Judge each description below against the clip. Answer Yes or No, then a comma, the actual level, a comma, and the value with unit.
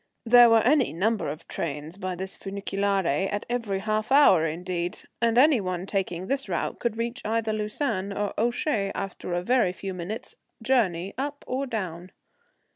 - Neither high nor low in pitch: No, high, 205 Hz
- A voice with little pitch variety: No, average, 4.3 semitones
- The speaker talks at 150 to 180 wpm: Yes, average, 165 wpm